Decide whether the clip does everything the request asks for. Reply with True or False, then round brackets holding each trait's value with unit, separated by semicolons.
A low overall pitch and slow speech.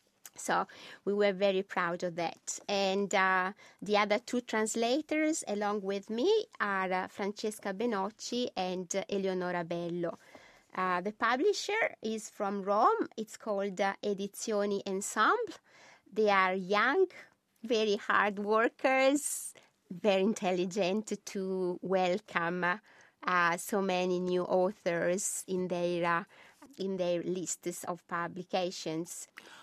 False (200 Hz; 115 wpm)